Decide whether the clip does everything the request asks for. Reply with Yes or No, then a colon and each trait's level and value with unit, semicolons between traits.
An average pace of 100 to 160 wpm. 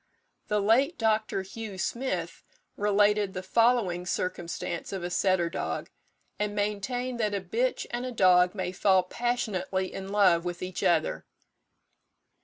Yes: average, 140 wpm